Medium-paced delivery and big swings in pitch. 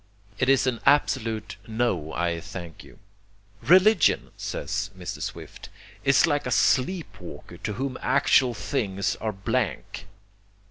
No: slow, 130 wpm; wide, 6.0 semitones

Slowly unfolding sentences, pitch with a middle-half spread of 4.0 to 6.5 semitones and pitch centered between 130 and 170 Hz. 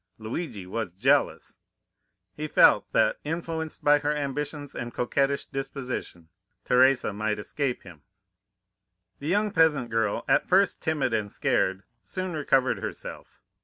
Yes: slow, 130 wpm; average, 5.3 semitones; low, 135 Hz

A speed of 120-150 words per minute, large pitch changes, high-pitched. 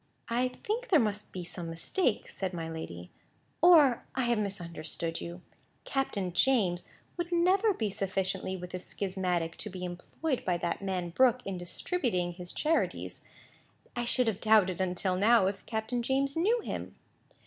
No: average, 160 wpm; wide, 6.1 semitones; high, 200 Hz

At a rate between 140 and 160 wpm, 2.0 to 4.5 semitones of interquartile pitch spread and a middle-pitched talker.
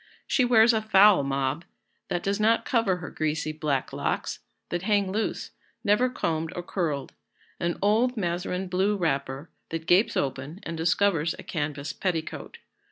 No: average, 155 wpm; average, 4.9 semitones; medium, 175 Hz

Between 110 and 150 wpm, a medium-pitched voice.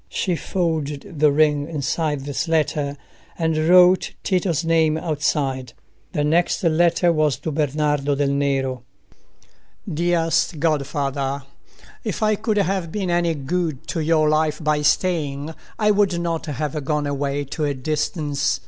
Yes: slow, 135 wpm; medium, 155 Hz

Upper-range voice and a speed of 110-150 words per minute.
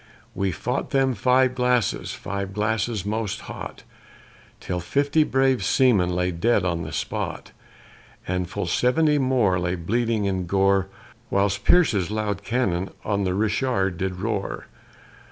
No: low, 100 Hz; average, 140 wpm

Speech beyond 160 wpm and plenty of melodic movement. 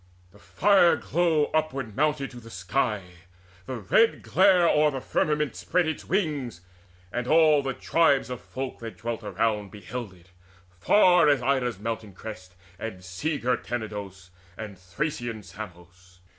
No: average, 145 wpm; wide, 7.2 semitones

